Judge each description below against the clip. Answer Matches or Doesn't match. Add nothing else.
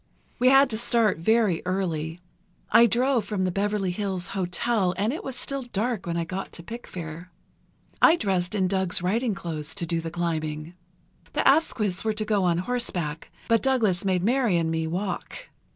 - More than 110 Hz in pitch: Matches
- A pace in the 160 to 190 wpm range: Matches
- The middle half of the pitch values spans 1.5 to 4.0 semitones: Doesn't match